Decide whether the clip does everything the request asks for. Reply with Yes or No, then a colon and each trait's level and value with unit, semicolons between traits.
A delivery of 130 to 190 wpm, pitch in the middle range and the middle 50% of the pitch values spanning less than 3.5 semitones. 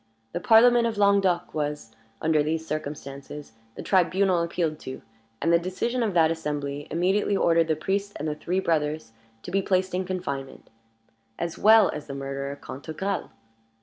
No: average, 160 wpm; medium, 165 Hz; average, 4.3 semitones